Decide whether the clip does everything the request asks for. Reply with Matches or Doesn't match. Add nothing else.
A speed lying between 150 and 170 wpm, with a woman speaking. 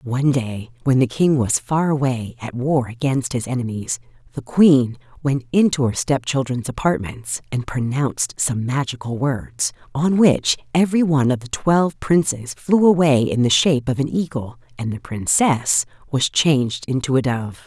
Matches